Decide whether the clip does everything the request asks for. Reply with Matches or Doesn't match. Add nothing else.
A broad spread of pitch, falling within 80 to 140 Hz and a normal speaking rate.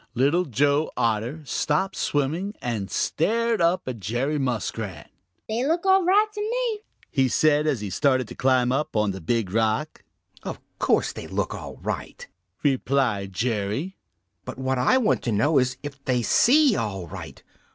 Matches